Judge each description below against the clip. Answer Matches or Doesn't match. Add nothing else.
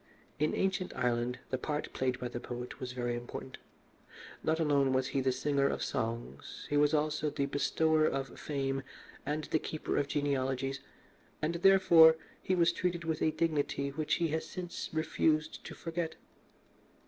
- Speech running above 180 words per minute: Doesn't match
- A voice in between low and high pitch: Matches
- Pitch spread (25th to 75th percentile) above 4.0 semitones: Doesn't match